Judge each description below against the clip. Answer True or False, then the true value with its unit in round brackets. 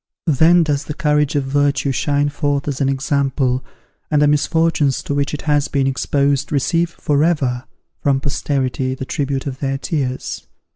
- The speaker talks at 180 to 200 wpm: False (165 wpm)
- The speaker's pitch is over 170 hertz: False (140 Hz)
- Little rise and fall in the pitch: True (1.6 semitones)